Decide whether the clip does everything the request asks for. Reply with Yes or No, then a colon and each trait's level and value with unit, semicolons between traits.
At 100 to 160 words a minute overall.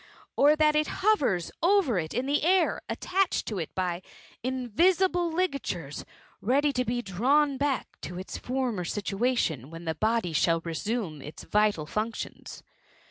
Yes: average, 140 wpm